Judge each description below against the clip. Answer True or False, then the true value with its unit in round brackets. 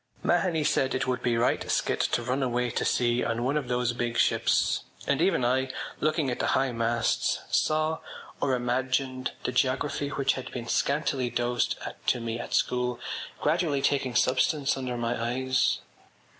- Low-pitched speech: True (125 Hz)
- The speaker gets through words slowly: False (170 wpm)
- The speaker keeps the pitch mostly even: True (2.2 semitones)